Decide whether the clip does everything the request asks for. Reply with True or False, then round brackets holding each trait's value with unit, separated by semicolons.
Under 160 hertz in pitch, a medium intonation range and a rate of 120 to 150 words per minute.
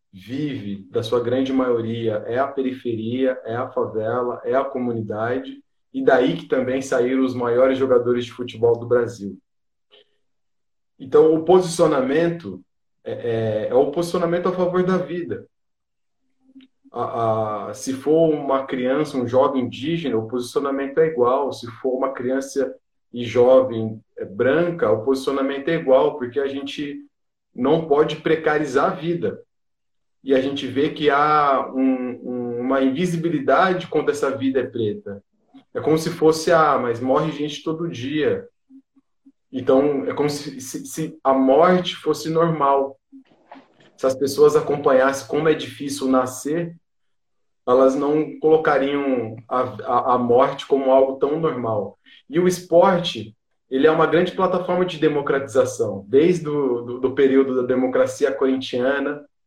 True (140 Hz; 4.8 semitones; 145 wpm)